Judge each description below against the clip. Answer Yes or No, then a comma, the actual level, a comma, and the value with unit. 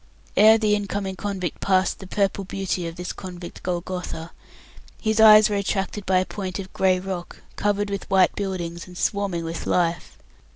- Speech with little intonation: Yes, narrow, 2.1 semitones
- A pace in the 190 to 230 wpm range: No, average, 175 wpm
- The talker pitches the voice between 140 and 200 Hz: Yes, high, 190 Hz